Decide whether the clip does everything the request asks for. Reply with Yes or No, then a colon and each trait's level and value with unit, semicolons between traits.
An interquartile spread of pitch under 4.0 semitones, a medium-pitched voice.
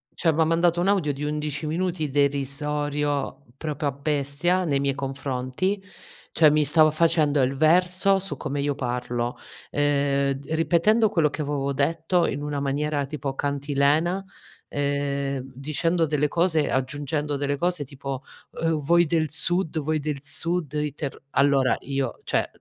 Yes: average, 2.7 semitones; medium, 145 Hz